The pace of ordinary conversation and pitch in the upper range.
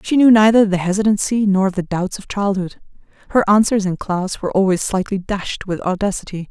Yes: average, 185 wpm; high, 195 Hz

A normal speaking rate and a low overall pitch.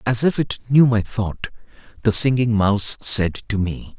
Yes: average, 180 wpm; low, 110 Hz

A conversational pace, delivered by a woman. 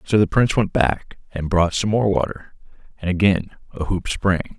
No: average, 195 wpm; male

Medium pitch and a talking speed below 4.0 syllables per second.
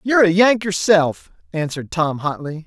No: medium, 175 Hz; 5.1 syllables/s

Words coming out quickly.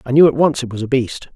Yes: fast, 355 wpm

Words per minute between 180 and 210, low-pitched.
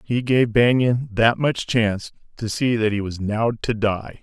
Yes: average, 200 wpm; low, 115 Hz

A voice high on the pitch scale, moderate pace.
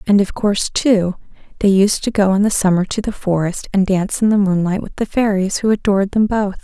No: high, 200 Hz; fast, 235 wpm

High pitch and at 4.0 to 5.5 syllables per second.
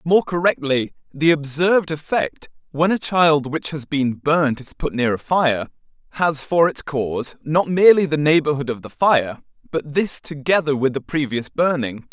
No: medium, 150 Hz; 4.6 syllables/s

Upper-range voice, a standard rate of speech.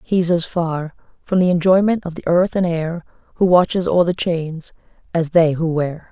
No: medium, 170 Hz; average, 195 wpm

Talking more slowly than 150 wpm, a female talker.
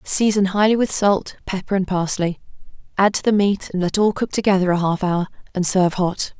No: fast, 205 wpm; female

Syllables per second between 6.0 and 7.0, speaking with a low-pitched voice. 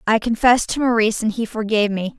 No: 6.8 syllables/s; high, 220 Hz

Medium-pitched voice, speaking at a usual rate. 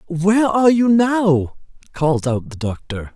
Yes: medium, 175 Hz; average, 150 wpm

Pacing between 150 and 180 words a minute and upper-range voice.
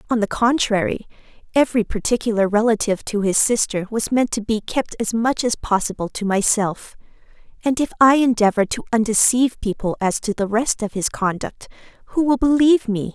Yes: average, 175 wpm; high, 225 Hz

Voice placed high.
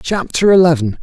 No: medium, 165 Hz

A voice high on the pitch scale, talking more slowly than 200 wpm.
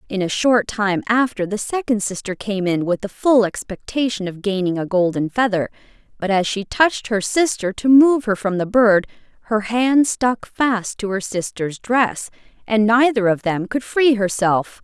Yes: high, 215 Hz; average, 185 wpm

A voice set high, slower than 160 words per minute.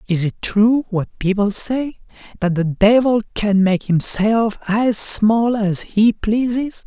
Yes: high, 215 Hz; average, 150 wpm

